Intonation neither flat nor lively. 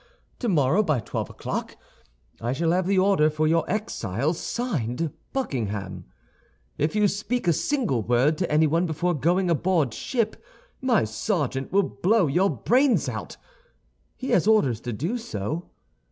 No: wide, 7.2 semitones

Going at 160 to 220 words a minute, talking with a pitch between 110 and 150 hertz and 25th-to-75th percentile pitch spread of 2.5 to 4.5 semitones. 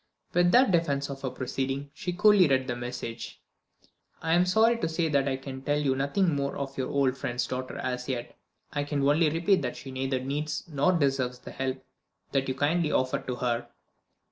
Yes: average, 200 wpm; medium, 140 Hz; average, 3.7 semitones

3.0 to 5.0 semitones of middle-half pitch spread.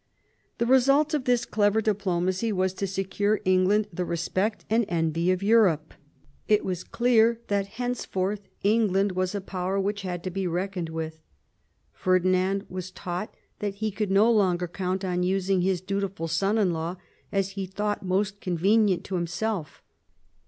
No: narrow, 2.4 semitones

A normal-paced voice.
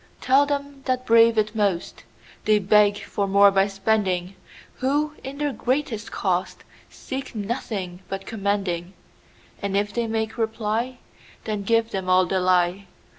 No: slow, 125 wpm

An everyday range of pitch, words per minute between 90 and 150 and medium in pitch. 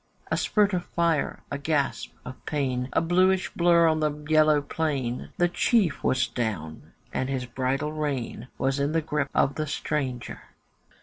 No: average, 3.8 semitones; average, 165 wpm; medium, 150 Hz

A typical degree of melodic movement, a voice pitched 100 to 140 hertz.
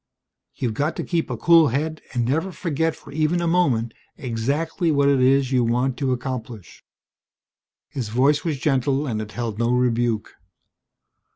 Yes: average, 4.3 semitones; low, 135 Hz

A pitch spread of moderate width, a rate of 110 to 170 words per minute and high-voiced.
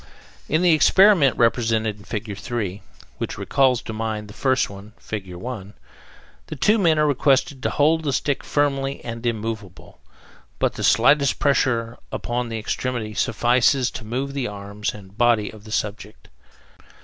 No: average, 4.5 semitones; average, 160 wpm; low, 120 Hz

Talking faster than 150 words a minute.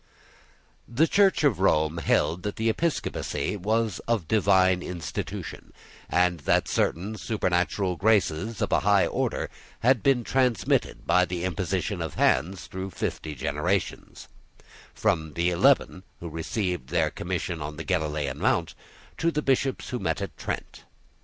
No: average, 140 wpm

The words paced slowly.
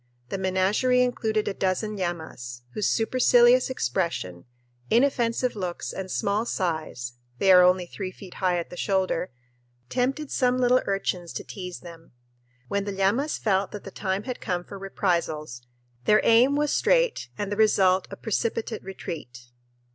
No: average, 155 wpm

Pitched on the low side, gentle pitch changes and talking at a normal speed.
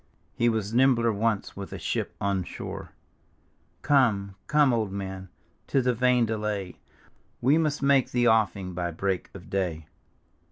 No: low, 110 Hz; average, 4.3 semitones; average, 155 wpm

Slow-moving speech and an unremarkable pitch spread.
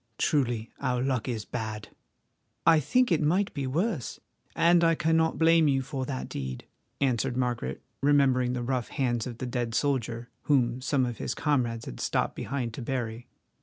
No: average, 170 wpm; average, 3.5 semitones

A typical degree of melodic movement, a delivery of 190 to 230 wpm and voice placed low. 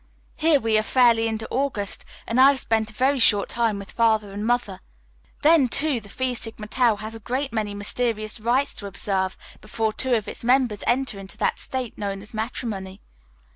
No: average, 3.3 semitones; average, 195 wpm; high, 225 Hz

